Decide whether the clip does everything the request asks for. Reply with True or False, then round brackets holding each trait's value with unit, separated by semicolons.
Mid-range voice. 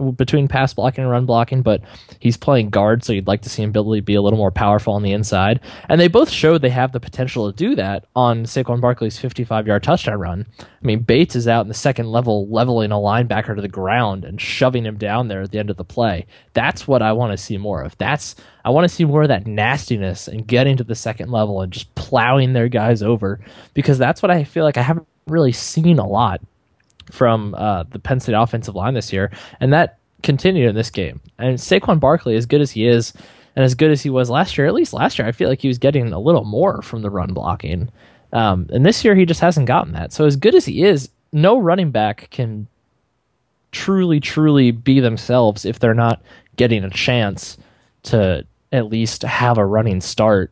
False (120 Hz)